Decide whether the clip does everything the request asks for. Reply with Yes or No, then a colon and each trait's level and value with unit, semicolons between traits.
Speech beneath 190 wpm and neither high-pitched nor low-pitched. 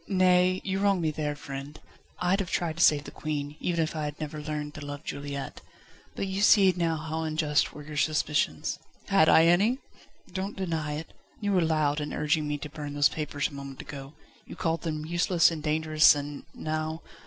No: average, 200 wpm; medium, 155 Hz